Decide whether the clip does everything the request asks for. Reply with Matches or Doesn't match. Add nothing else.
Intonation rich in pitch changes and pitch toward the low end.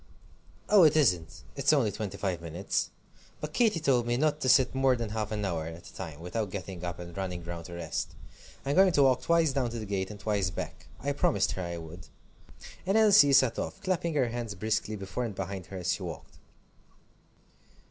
Matches